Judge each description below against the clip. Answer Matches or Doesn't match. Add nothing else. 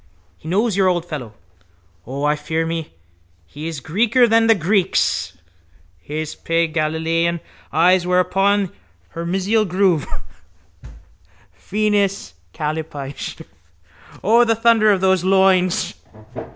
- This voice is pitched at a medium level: Matches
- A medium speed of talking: Doesn't match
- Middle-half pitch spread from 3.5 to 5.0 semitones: Matches